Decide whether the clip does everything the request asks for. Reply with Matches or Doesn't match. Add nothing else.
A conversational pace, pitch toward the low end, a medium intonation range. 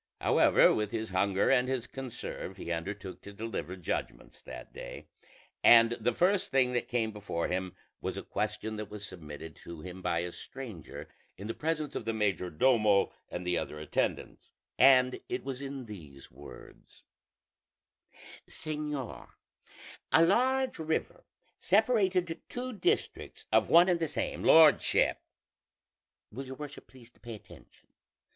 Doesn't match